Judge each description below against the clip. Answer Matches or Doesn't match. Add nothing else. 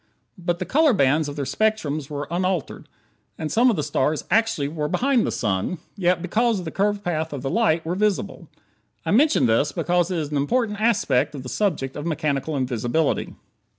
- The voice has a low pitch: Doesn't match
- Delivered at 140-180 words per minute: Doesn't match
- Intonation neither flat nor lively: Doesn't match